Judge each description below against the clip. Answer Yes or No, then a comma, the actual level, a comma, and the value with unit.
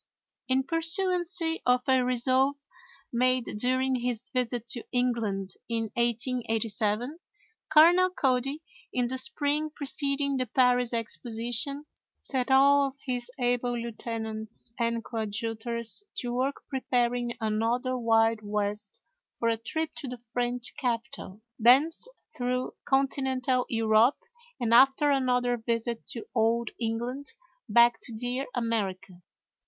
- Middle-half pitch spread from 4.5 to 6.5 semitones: No, narrow, 2.5 semitones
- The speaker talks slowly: Yes, slow, 115 wpm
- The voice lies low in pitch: No, high, 245 Hz